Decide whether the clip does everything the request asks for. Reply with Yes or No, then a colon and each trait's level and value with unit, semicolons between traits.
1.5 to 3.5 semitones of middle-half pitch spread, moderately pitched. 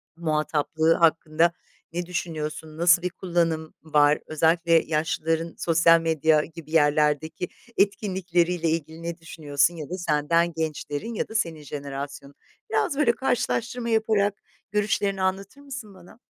Yes: average, 2.9 semitones; medium, 165 Hz